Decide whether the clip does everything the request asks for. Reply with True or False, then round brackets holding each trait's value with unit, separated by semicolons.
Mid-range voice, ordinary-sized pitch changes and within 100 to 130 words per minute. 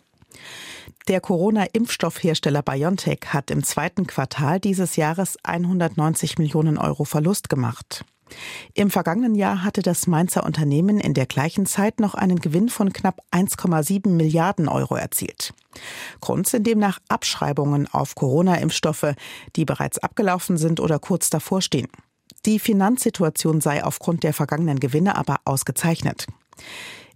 True (165 Hz; 4.3 semitones; 125 wpm)